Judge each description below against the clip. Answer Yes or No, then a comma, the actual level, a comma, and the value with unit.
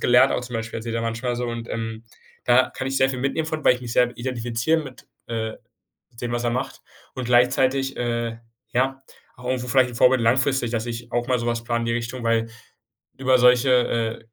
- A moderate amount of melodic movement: No, narrow, 1.7 semitones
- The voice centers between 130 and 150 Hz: No, low, 120 Hz